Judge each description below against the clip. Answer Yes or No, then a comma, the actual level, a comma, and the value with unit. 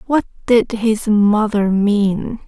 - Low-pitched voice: No, high, 215 Hz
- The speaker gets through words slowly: Yes, slow, 120 wpm